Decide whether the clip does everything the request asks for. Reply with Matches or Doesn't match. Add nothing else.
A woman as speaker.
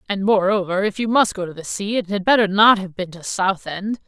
Matches